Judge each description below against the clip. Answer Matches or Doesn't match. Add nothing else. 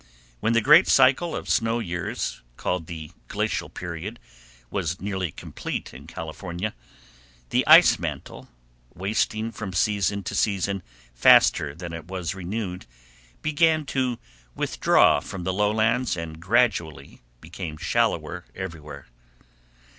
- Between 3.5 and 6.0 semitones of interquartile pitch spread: Matches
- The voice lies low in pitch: Matches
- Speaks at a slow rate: Matches